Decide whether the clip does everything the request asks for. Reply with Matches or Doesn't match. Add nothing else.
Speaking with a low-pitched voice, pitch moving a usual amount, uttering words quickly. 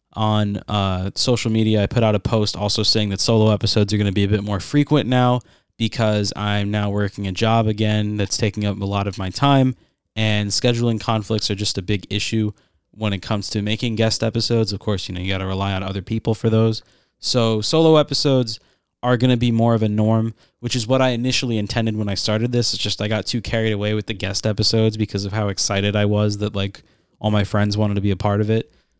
Doesn't match